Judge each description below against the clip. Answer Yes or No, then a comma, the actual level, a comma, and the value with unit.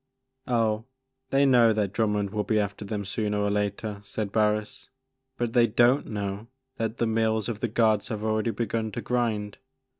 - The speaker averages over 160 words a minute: Yes, average, 180 wpm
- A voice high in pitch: No, low, 110 Hz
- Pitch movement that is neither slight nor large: No, narrow, 2.0 semitones